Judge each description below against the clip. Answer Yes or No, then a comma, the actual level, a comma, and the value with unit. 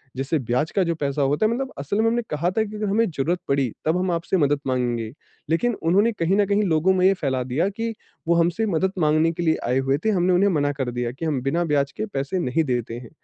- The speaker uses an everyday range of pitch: No, wide, 5.7 semitones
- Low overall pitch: No, medium, 165 Hz